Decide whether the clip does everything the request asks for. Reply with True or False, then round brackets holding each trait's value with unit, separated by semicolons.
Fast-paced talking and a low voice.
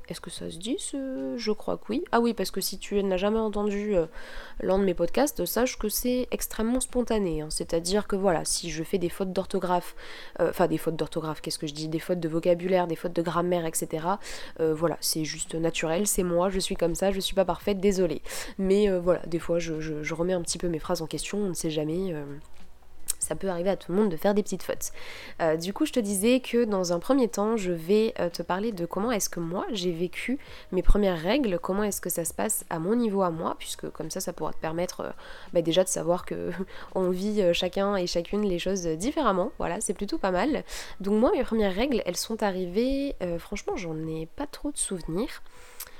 False (240 wpm; 190 Hz)